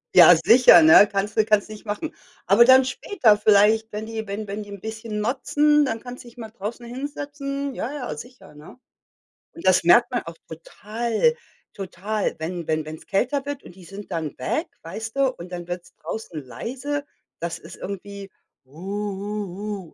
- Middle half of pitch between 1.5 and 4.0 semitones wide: No, average, 4.4 semitones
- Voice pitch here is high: Yes, high, 215 Hz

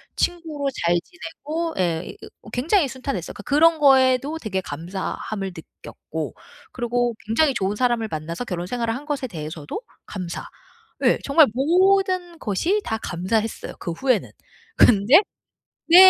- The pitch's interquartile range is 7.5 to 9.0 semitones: Yes, wide, 8.1 semitones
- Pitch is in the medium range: No, high, 245 Hz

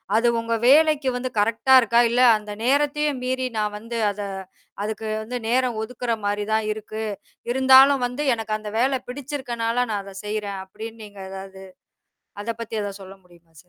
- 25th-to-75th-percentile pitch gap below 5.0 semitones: Yes, average, 3.5 semitones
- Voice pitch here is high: Yes, high, 230 Hz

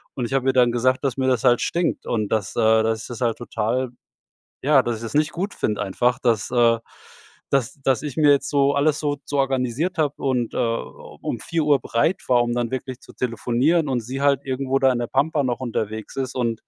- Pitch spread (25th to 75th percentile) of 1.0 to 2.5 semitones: No, average, 2.9 semitones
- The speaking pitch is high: No, low, 130 Hz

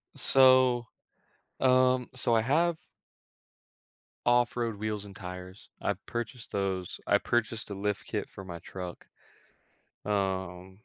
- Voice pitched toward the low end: Yes, low, 105 Hz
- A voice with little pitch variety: No, average, 4.3 semitones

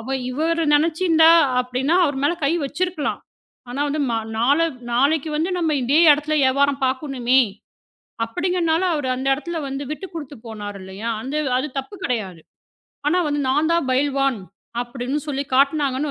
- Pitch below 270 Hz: No, very high, 280 Hz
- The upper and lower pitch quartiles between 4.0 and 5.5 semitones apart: No, average, 3.5 semitones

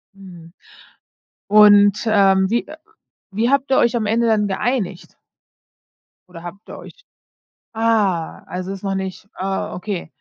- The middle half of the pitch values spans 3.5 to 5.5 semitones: No, average, 2.9 semitones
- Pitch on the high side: Yes, high, 200 Hz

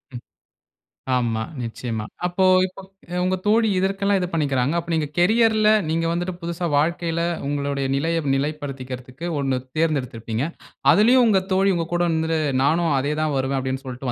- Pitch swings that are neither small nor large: Yes, average, 5.0 semitones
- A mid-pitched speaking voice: Yes, medium, 160 Hz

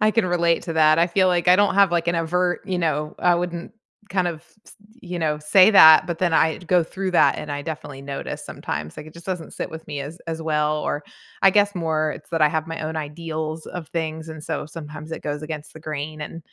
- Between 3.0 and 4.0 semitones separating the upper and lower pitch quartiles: No, narrow, 2.4 semitones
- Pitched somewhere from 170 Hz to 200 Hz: No, medium, 160 Hz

